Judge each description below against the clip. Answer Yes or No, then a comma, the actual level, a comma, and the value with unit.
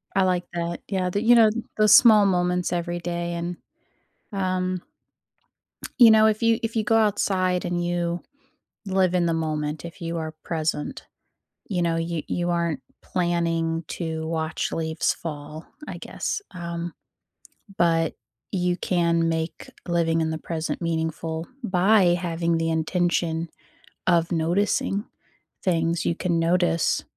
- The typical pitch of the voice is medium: Yes, medium, 170 Hz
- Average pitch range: No, narrow, 1.9 semitones